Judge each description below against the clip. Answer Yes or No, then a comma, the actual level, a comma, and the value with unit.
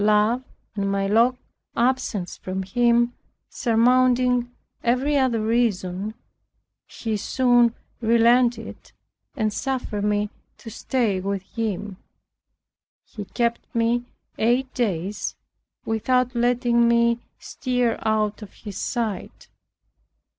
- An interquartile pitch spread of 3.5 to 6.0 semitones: No, average, 2.7 semitones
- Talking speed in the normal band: No, slow, 100 wpm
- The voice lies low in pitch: No, high, 235 Hz